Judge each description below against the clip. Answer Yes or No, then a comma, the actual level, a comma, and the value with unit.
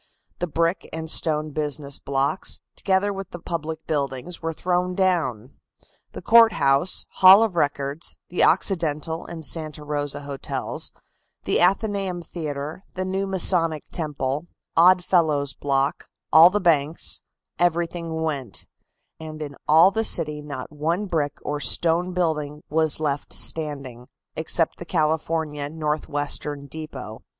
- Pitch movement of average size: Yes, average, 3.3 semitones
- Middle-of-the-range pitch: Yes, medium, 160 Hz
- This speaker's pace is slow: Yes, slow, 130 wpm